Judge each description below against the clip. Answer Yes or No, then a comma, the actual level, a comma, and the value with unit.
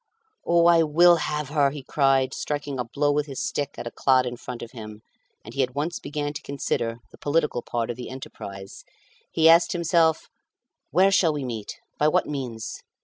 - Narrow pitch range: No, average, 4.0 semitones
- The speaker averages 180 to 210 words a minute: Yes, average, 200 wpm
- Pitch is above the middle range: No, medium, 140 Hz